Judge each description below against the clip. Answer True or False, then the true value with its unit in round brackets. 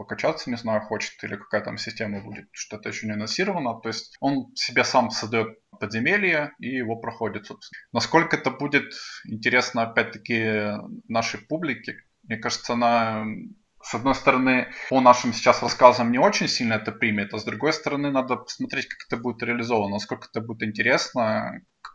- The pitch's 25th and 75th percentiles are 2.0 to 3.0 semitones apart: True (2.6 semitones)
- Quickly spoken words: True (165 wpm)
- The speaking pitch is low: True (120 Hz)